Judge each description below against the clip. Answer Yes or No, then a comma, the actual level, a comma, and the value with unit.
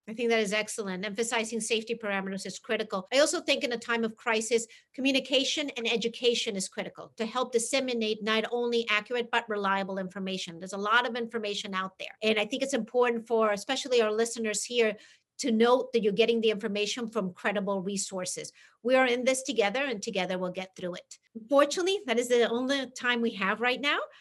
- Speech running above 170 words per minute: Yes, average, 200 wpm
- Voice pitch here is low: No, high, 230 Hz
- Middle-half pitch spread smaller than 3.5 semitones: Yes, average, 2.9 semitones